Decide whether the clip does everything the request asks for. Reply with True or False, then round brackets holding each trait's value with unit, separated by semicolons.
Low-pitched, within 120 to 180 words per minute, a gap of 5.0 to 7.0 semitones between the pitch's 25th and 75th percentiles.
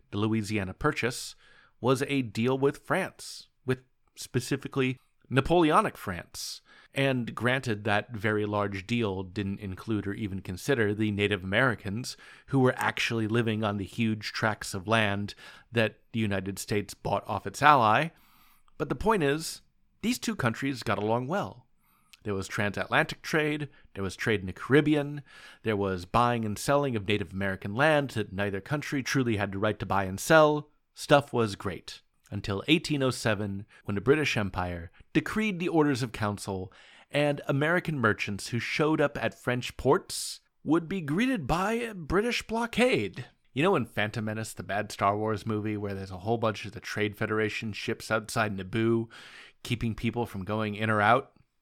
True (115 Hz; 165 wpm; 5.3 semitones)